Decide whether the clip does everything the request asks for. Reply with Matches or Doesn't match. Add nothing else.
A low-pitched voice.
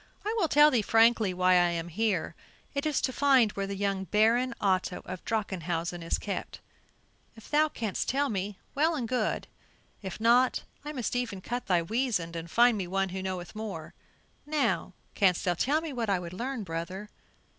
Doesn't match